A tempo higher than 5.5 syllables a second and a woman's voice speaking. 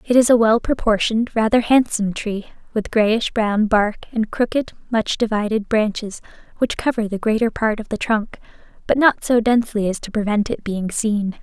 No: 5.1 syllables/s; female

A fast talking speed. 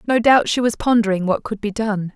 Yes: fast, 250 wpm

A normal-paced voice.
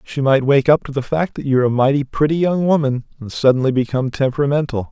No: fast, 220 wpm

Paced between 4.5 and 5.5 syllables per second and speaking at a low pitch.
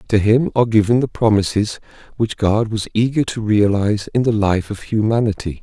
Yes: 5.4 syllables/s; low, 110 Hz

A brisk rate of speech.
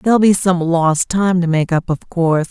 Yes: fast, 240 wpm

